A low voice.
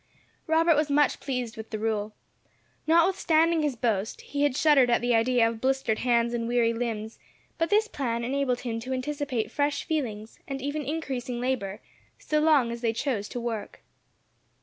No: very high, 250 Hz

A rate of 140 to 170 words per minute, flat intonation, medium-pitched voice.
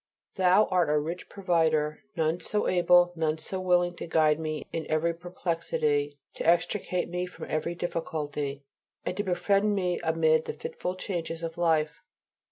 Yes: average, 160 wpm; narrow, 2.3 semitones; medium, 170 Hz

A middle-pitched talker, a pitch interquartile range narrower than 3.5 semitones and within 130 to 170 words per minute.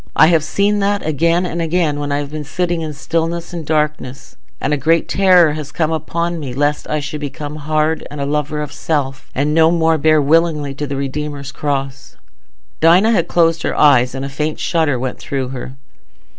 No: medium, 150 Hz; narrow, 2.5 semitones; average, 200 wpm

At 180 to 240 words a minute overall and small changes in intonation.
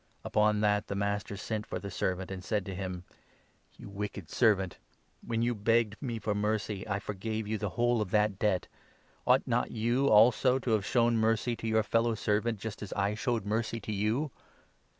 Yes: fast, 205 wpm; narrow, 2.1 semitones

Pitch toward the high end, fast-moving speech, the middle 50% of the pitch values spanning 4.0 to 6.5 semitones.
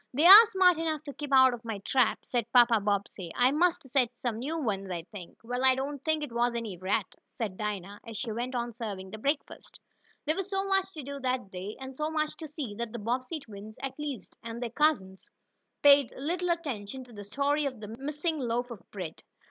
Yes: very high, 250 Hz; fast, 220 wpm; wide, 5.4 semitones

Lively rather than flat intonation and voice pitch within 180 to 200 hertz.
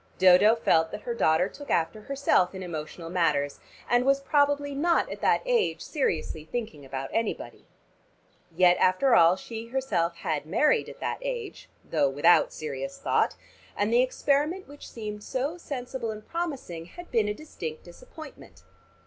No: wide, 8.8 semitones; high, 215 Hz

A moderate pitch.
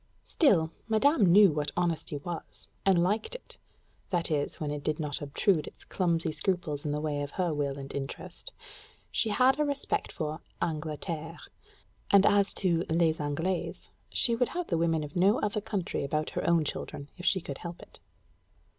Yes: medium, 165 Hz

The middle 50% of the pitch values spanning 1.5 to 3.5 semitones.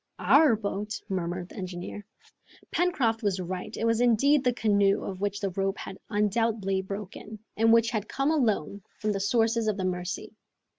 Yes: average, 2.9 semitones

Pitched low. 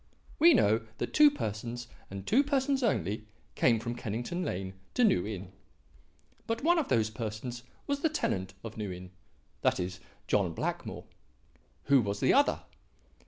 Yes: low, 115 Hz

